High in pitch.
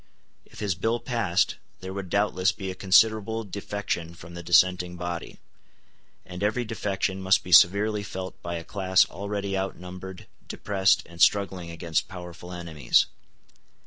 No: very low, 95 Hz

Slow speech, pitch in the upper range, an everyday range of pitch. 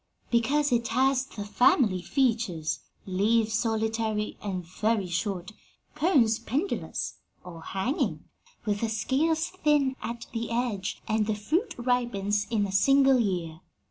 Yes: slow, 130 wpm; high, 225 Hz; average, 4.2 semitones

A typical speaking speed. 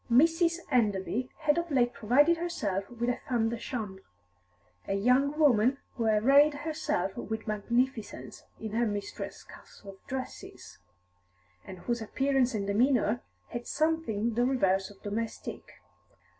No: slow, 130 wpm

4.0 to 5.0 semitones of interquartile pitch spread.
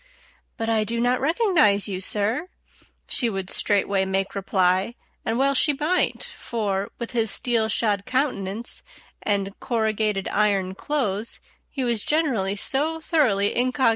Yes: average, 4.5 semitones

